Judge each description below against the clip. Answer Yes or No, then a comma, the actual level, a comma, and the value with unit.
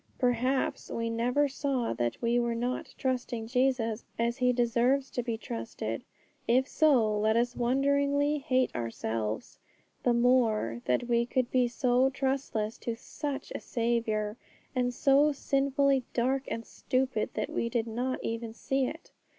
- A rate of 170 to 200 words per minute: No, average, 150 wpm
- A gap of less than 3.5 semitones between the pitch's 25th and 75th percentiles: Yes, narrow, 2.6 semitones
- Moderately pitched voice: No, high, 245 Hz